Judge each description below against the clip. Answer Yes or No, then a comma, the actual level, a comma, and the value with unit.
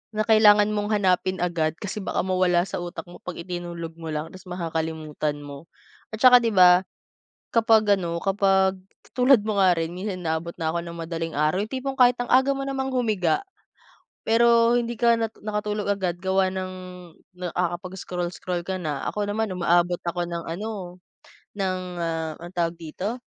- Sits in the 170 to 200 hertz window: Yes, medium, 185 Hz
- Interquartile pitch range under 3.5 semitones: No, average, 3.8 semitones